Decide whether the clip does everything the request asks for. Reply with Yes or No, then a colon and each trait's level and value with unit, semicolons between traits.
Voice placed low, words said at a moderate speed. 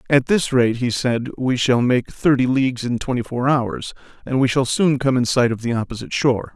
No: low, 125 Hz; fast, 230 wpm